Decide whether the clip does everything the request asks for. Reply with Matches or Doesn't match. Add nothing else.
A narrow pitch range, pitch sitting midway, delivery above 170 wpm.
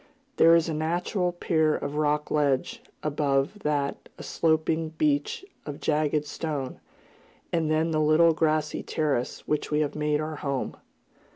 Doesn't match